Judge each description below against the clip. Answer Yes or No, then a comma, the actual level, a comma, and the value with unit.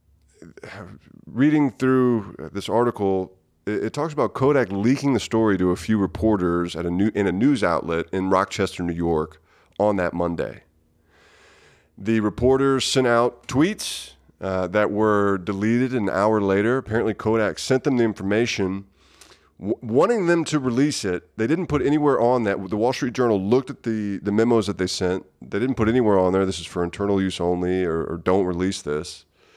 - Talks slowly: No, average, 180 wpm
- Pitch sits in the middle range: No, low, 100 Hz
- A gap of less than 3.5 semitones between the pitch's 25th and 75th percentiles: No, average, 4.4 semitones